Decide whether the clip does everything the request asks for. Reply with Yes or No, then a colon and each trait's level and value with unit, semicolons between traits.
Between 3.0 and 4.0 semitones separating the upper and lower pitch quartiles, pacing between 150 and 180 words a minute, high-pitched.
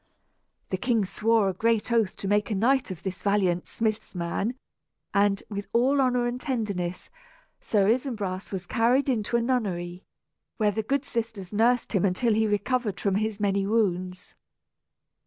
Yes: average, 3.4 semitones; average, 160 wpm; high, 210 Hz